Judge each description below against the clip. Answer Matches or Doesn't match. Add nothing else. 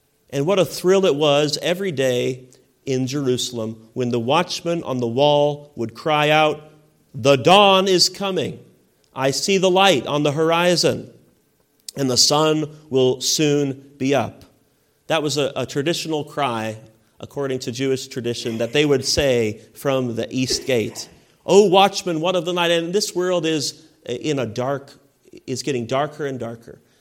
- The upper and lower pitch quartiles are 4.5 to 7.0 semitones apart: Doesn't match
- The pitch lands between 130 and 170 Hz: Matches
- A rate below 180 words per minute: Matches